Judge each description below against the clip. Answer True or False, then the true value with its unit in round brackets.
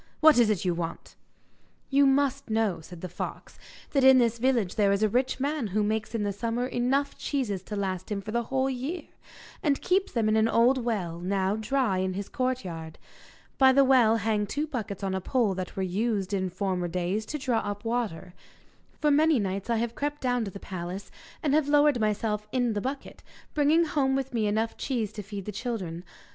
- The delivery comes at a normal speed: False (210 wpm)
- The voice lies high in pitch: True (225 Hz)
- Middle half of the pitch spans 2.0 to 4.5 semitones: False (5.0 semitones)